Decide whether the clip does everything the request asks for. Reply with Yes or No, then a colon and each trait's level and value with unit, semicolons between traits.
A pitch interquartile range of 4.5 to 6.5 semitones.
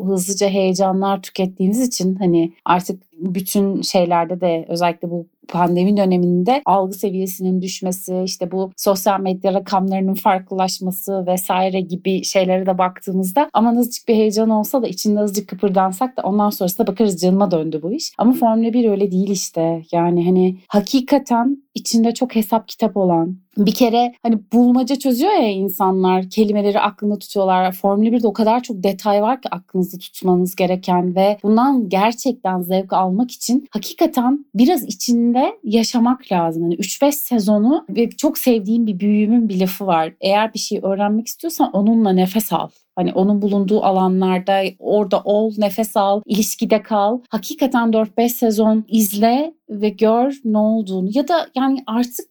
No: average, 3.6 semitones